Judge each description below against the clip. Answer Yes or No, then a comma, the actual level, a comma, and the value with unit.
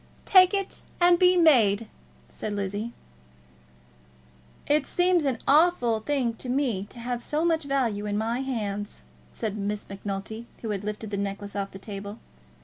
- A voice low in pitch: No, high, 230 Hz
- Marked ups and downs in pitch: Yes, wide, 5.9 semitones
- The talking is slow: No, average, 155 wpm